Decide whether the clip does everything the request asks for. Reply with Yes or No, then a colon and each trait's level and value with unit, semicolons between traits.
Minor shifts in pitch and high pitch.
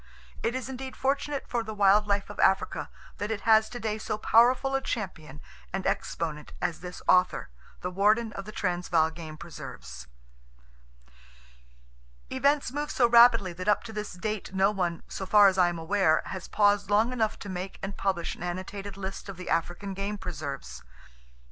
No: average, 3.5 semitones; high, 200 Hz